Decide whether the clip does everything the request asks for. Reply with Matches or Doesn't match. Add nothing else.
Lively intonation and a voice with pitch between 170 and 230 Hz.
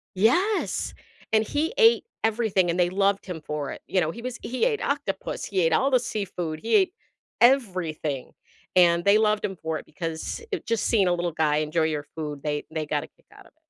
Matches